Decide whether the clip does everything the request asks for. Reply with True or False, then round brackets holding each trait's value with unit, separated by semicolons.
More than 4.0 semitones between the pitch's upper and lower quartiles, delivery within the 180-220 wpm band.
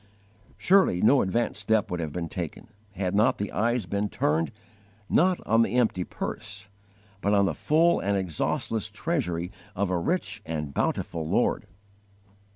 False (4.6 semitones; 160 wpm)